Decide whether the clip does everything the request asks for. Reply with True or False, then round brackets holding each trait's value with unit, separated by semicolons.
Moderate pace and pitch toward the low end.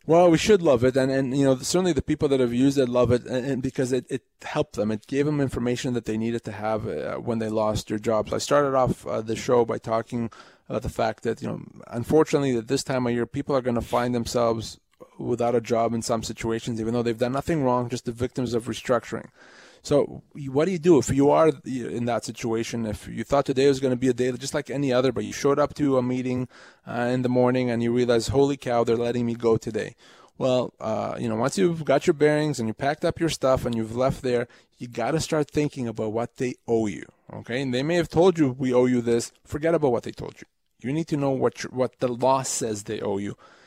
False (255 wpm; 125 Hz)